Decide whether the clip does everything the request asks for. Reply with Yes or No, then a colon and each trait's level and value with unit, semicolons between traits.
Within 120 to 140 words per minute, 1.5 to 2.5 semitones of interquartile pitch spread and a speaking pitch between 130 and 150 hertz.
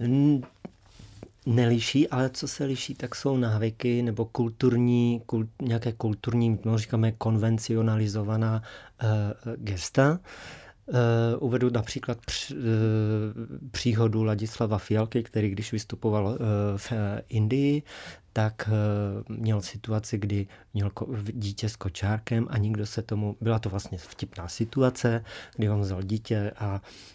No: average, 125 wpm; narrow, 2.0 semitones; low, 110 Hz